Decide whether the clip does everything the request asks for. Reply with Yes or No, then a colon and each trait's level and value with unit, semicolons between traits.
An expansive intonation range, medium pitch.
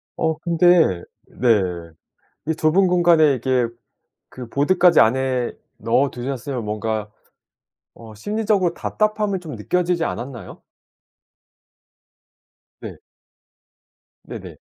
Yes: wide, 6.6 semitones; medium, 145 Hz